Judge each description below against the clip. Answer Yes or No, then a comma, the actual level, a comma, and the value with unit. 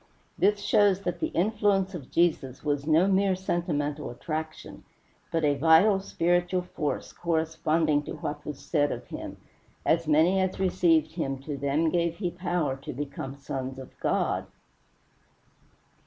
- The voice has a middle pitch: Yes, medium, 160 Hz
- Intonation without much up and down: No, average, 3.5 semitones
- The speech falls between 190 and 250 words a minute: No, average, 145 wpm